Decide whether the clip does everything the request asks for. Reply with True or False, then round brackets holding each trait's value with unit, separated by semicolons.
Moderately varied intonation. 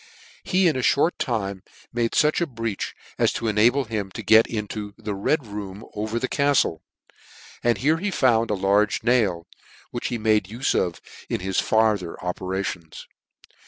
True (3.6 semitones)